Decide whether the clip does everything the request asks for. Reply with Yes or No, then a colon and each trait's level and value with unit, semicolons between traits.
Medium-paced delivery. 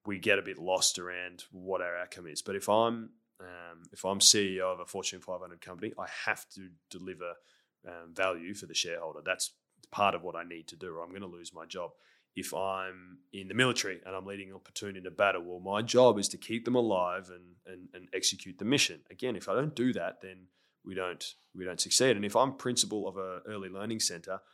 No: fast, 225 wpm